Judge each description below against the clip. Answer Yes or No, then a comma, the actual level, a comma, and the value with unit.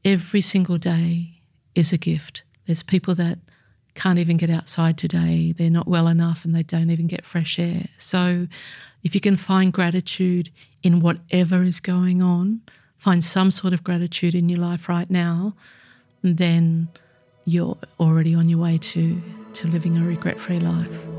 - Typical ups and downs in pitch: No, narrow, 1.5 semitones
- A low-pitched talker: No, medium, 170 Hz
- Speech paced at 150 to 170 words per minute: Yes, average, 165 wpm